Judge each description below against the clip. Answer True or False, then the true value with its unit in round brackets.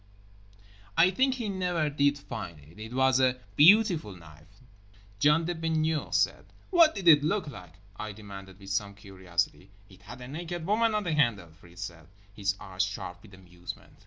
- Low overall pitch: True (120 Hz)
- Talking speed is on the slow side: False (175 wpm)